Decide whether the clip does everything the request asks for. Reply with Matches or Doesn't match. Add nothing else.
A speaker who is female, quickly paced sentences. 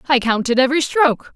Doesn't match